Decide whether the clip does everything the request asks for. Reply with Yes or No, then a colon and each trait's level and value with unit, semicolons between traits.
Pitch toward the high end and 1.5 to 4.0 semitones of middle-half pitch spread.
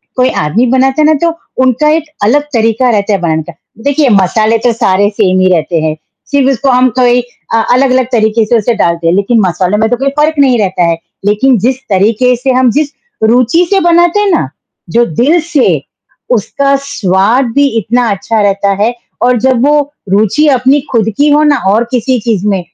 No: high, 240 Hz; average, 4.8 semitones